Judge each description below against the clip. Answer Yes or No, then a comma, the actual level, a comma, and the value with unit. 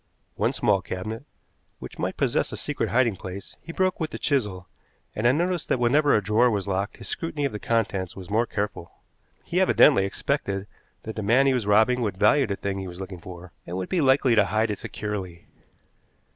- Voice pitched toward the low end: Yes, low, 105 Hz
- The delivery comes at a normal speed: No, fast, 210 wpm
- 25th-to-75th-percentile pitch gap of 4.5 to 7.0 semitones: Yes, average, 5.1 semitones